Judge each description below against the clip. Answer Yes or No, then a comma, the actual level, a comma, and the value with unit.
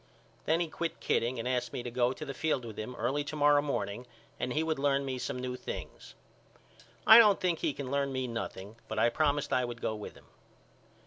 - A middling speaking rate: No, fast, 220 wpm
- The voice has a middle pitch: No, low, 130 Hz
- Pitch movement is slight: No, average, 3.4 semitones